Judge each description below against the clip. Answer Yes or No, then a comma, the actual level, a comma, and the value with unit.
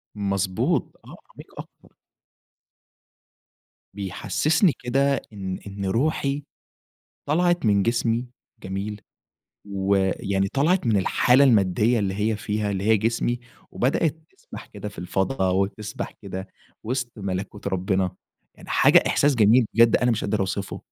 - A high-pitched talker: No, low, 105 Hz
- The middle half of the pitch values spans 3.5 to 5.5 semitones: Yes, average, 4.0 semitones